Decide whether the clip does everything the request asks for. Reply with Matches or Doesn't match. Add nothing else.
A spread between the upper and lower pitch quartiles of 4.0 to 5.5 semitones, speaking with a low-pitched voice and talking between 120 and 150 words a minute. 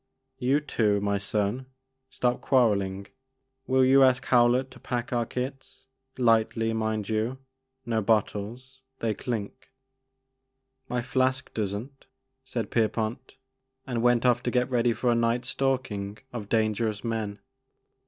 Doesn't match